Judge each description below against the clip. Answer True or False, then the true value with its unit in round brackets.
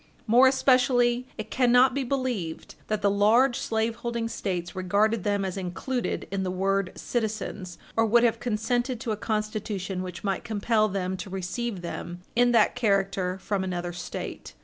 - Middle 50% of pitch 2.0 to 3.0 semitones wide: False (4.0 semitones)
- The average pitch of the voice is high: True (215 Hz)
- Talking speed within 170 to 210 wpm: False (160 wpm)